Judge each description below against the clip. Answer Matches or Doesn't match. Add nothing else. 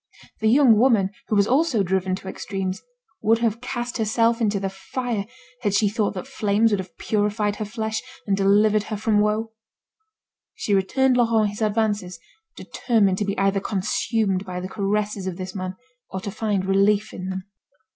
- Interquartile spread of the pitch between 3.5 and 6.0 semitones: Doesn't match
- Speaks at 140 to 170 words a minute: Doesn't match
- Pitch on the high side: Matches